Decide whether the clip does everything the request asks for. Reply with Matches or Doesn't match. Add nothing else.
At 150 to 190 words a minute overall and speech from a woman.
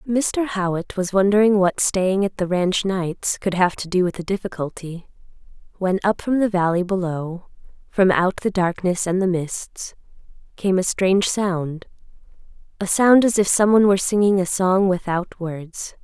Matches